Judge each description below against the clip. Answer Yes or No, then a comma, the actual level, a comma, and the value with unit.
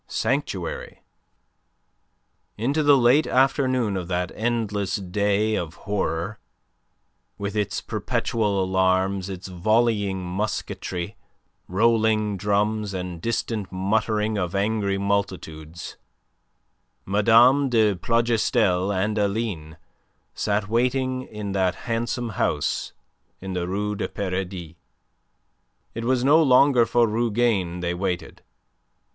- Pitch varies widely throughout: No, average, 3.6 semitones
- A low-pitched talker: Yes, low, 105 Hz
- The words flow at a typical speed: No, slow, 105 wpm